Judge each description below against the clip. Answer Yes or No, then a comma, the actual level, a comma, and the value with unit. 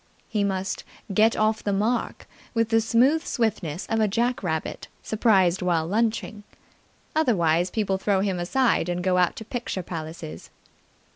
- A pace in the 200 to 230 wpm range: No, average, 150 wpm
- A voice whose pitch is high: Yes, high, 200 Hz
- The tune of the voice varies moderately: Yes, average, 4.1 semitones